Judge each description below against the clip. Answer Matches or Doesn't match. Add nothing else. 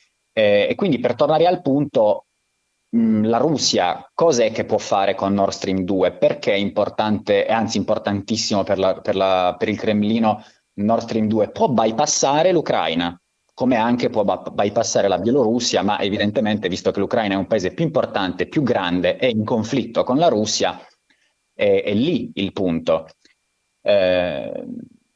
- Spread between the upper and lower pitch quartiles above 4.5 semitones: Doesn't match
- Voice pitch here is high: Doesn't match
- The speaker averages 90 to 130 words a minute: Doesn't match